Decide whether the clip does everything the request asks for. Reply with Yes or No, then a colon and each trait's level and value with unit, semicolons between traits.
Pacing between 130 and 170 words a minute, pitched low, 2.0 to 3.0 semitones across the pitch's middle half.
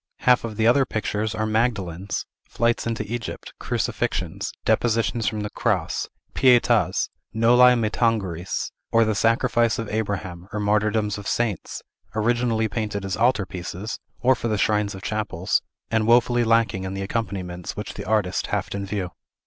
Yes: average, 155 wpm; low, 110 Hz; average, 2.7 semitones